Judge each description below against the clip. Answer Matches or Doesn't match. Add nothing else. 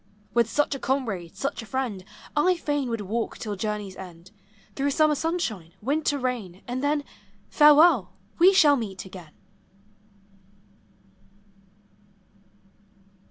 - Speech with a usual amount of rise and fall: Doesn't match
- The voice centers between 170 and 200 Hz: Doesn't match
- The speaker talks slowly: Matches